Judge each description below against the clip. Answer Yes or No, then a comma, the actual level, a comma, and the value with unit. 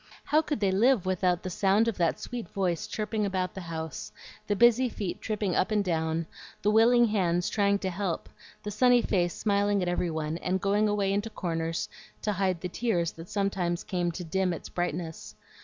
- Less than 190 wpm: No, average, 195 wpm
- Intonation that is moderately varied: Yes, average, 3.2 semitones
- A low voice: No, high, 190 Hz